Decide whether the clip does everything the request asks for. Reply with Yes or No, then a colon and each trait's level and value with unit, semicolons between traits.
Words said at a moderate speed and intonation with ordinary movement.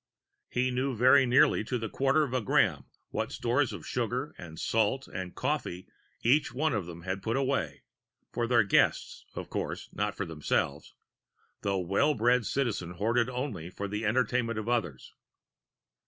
Yes: average, 165 wpm; average, 4.5 semitones